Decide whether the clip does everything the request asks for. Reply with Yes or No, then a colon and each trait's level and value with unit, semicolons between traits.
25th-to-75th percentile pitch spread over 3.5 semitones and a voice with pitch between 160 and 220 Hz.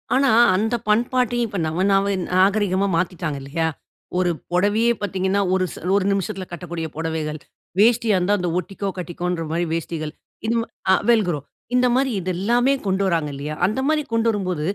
Yes: average, 4.3 semitones; high, 190 Hz